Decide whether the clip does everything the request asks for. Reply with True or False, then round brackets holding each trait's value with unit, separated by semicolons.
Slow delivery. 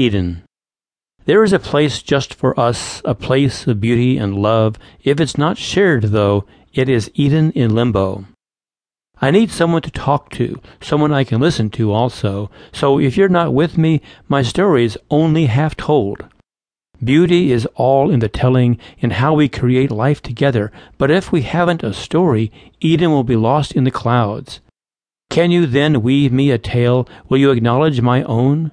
False (180 wpm)